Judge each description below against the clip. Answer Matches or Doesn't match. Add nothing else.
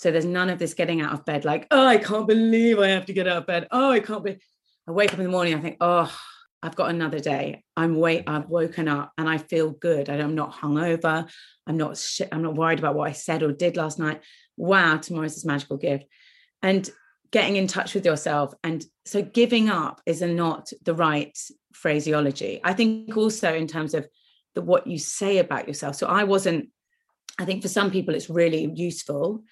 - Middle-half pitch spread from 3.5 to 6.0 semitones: Matches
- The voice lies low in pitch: Doesn't match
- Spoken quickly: Matches